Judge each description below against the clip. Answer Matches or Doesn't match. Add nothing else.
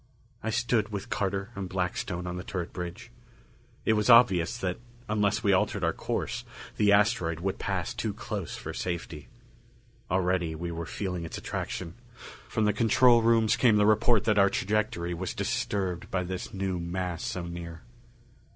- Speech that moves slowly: Doesn't match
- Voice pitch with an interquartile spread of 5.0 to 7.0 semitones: Doesn't match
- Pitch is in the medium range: Doesn't match